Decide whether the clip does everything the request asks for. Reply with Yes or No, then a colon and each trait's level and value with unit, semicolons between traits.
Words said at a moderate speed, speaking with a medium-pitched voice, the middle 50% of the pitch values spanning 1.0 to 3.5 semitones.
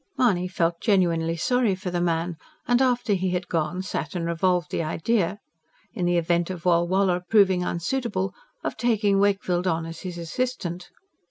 Yes: average, 165 wpm; medium, 180 Hz; average, 2.7 semitones